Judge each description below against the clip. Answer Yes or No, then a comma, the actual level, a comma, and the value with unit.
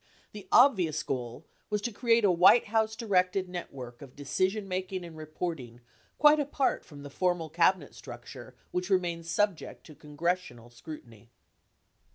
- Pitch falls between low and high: Yes, medium, 180 Hz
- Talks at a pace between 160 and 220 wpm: No, average, 145 wpm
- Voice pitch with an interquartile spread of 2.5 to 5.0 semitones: No, wide, 5.4 semitones